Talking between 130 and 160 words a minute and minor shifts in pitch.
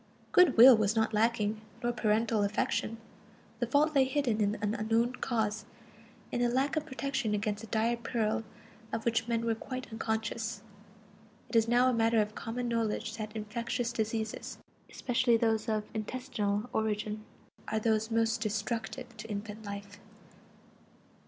Yes: average, 150 wpm; narrow, 1.8 semitones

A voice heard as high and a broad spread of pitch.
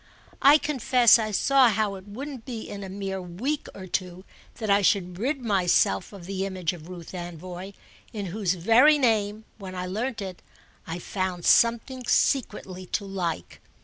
No: high, 200 Hz; average, 4.1 semitones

